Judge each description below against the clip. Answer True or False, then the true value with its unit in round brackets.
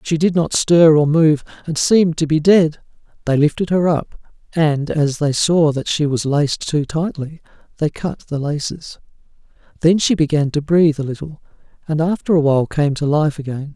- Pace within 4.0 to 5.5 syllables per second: True (5.0 syllables/s)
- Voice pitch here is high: False (155 Hz)